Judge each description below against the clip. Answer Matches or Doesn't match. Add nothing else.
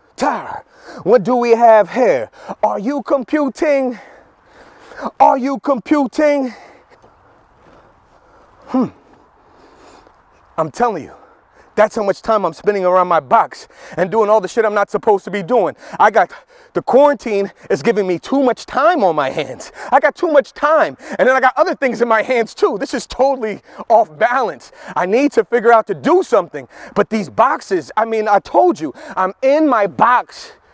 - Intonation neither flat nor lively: Matches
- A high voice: Matches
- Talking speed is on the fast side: Doesn't match